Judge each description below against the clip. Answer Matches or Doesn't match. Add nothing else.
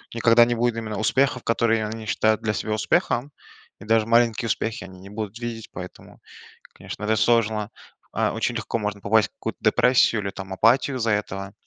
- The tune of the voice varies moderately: Doesn't match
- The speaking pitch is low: Matches